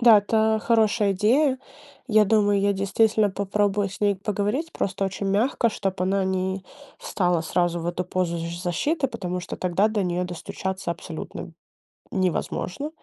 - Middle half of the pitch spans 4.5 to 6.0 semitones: No, average, 2.9 semitones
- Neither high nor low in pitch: No, high, 195 Hz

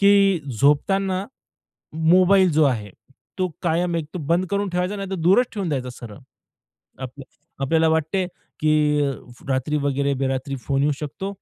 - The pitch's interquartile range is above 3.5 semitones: Yes, average, 5.2 semitones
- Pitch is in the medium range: Yes, medium, 160 Hz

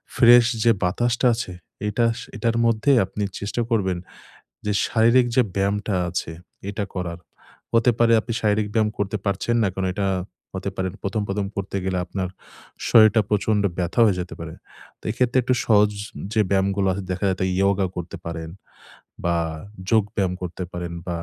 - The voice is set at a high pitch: No, low, 100 Hz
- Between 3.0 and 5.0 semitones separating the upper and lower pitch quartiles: Yes, average, 3.3 semitones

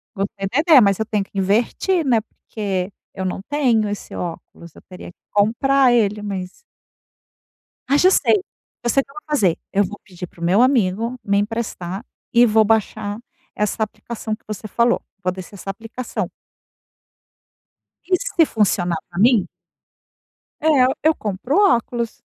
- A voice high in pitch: Yes, high, 215 Hz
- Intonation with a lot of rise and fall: No, average, 3.8 semitones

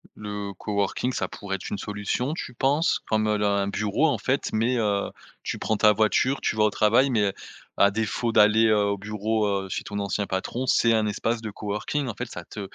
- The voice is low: Yes, low, 105 Hz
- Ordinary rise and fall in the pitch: No, narrow, 2.2 semitones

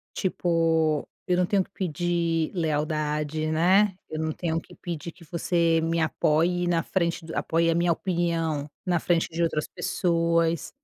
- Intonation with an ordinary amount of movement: No, narrow, 1.6 semitones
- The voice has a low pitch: No, medium, 165 Hz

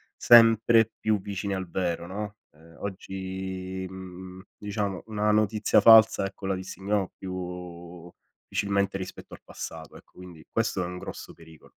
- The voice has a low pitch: Yes, very low, 95 Hz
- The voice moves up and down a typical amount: No, narrow, 2.3 semitones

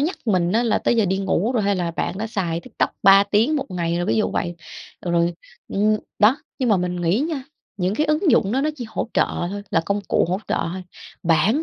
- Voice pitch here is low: No, high, 200 Hz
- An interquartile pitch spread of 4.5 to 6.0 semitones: Yes, average, 4.8 semitones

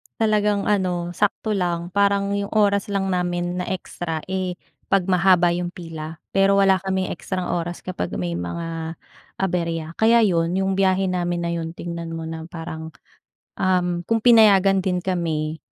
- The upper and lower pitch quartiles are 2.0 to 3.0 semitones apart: Yes, narrow, 2.5 semitones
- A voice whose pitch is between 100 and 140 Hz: No, medium, 180 Hz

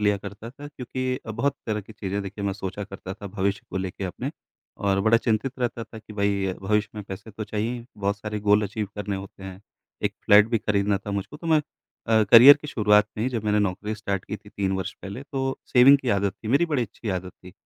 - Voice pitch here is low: Yes, low, 105 Hz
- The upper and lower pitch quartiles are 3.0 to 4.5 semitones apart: No, narrow, 2.6 semitones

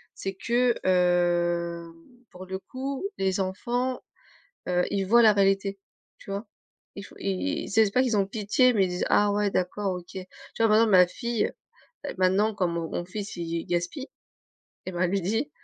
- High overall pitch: Yes, high, 195 Hz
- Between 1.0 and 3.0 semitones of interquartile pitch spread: No, average, 3.5 semitones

